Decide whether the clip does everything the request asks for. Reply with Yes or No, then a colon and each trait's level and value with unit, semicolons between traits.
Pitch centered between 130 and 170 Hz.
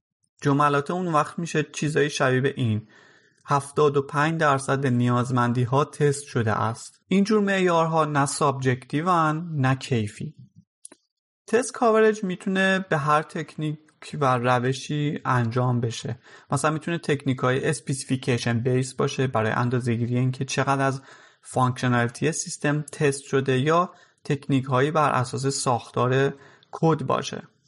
Yes: medium, 140 Hz